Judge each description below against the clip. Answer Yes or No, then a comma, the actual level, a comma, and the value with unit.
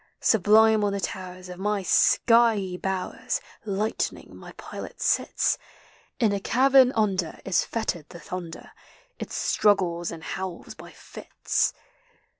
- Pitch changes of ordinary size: Yes, average, 3.2 semitones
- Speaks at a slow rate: Yes, slow, 125 wpm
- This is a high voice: Yes, high, 195 Hz